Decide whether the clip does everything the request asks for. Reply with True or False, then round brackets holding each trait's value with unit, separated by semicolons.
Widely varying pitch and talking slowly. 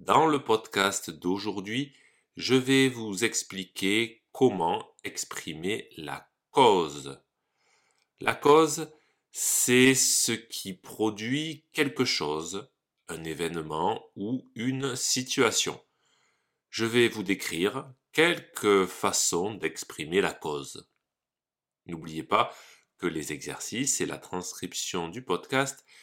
True (6.4 semitones; 100 wpm)